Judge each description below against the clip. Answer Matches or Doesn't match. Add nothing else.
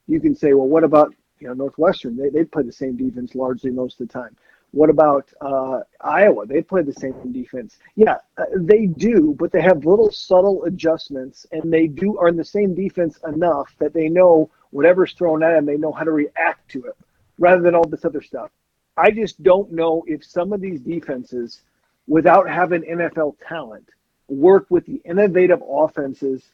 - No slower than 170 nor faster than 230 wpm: Matches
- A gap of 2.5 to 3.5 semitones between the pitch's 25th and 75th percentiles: Doesn't match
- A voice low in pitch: Doesn't match